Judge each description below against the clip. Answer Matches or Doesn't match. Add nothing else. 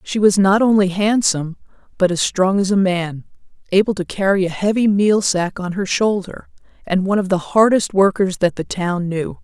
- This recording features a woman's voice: Matches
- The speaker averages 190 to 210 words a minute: Matches